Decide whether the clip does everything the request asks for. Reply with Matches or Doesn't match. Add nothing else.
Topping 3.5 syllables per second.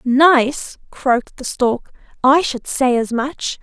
Doesn't match